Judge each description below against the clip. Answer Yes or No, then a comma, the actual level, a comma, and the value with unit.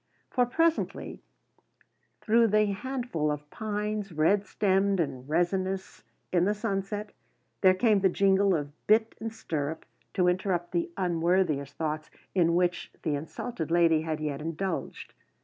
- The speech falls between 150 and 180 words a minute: No, slow, 135 wpm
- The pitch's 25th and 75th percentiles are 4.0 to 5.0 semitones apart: Yes, average, 4.5 semitones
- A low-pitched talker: No, medium, 185 Hz